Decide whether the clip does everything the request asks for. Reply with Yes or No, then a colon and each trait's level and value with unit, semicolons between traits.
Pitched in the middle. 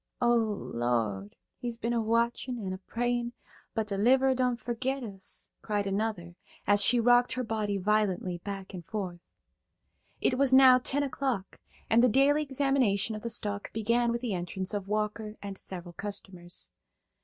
No: high, 220 Hz